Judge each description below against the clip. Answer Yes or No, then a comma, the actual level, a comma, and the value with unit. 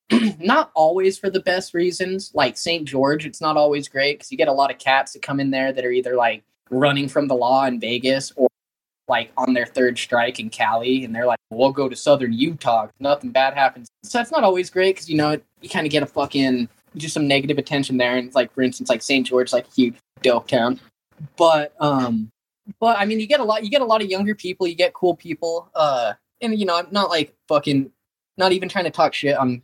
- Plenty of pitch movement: Yes, wide, 5.8 semitones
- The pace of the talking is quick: Yes, fast, 245 wpm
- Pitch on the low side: No, medium, 145 Hz